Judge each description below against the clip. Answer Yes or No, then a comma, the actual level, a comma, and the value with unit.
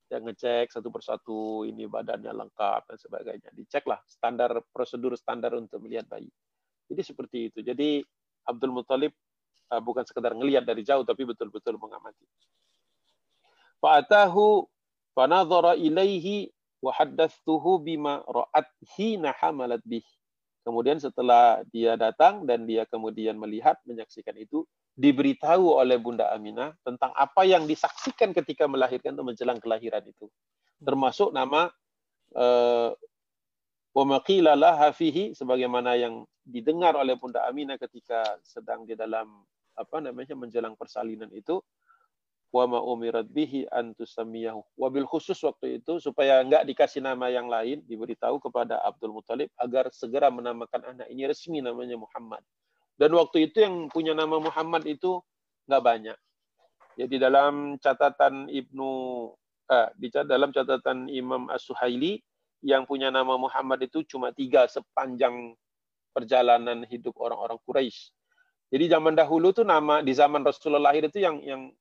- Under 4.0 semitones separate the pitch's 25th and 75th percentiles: No, average, 4.8 semitones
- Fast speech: No, average, 130 wpm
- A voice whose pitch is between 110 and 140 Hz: Yes, low, 135 Hz